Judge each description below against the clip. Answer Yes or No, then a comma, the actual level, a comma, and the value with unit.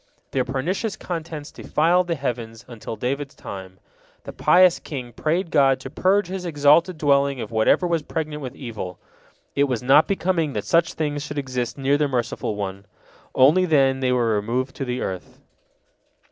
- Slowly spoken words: No, average, 170 wpm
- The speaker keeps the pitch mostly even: No, average, 4.7 semitones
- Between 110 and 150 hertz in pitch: Yes, medium, 140 Hz